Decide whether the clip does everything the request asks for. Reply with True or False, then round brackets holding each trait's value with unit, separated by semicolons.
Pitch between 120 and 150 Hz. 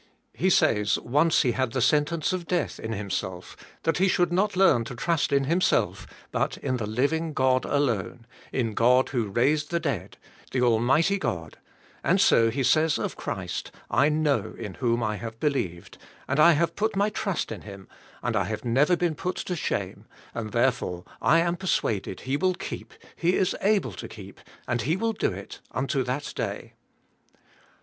True (135 Hz)